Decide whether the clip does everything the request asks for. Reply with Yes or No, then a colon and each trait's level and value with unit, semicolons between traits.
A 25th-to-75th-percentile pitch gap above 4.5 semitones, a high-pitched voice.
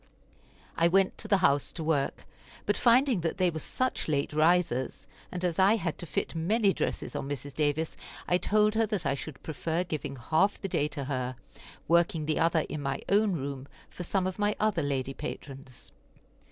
No: average, 5.3 semitones; medium, 165 Hz